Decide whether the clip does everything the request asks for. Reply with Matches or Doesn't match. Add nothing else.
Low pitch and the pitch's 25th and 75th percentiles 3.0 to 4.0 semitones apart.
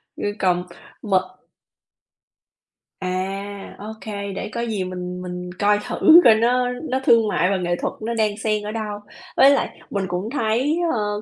Doesn't match